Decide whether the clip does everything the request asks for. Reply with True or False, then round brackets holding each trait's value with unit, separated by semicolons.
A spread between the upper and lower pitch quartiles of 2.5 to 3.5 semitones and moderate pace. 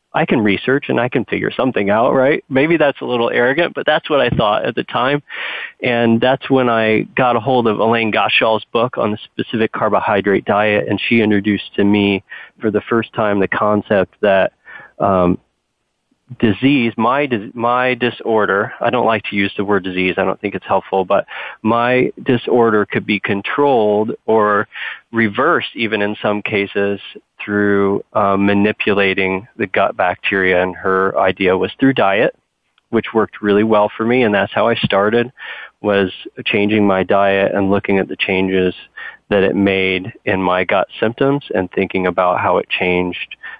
True (3.2 semitones; 175 wpm)